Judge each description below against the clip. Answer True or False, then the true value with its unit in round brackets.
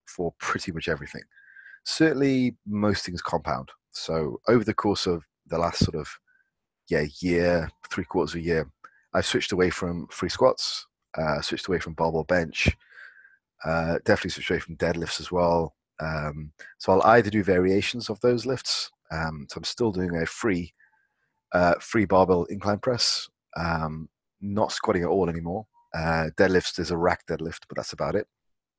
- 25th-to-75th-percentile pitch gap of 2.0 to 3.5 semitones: False (4.6 semitones)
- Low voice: True (90 Hz)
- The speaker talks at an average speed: True (170 wpm)